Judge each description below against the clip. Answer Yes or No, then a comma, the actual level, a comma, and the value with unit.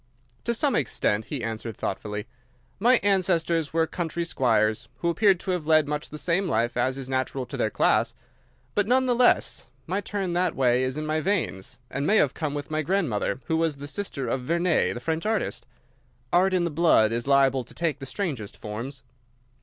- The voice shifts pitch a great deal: Yes, wide, 5.8 semitones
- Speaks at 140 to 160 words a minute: No, average, 200 wpm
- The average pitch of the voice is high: No, medium, 155 Hz